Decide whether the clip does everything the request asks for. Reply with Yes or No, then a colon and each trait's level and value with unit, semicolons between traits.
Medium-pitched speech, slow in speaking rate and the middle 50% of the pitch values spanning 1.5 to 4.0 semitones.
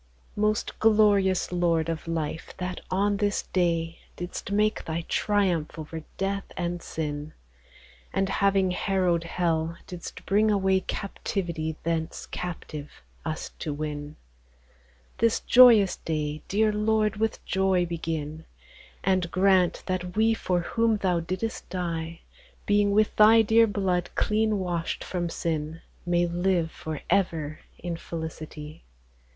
Yes: medium, 180 Hz; slow, 125 wpm; average, 3.6 semitones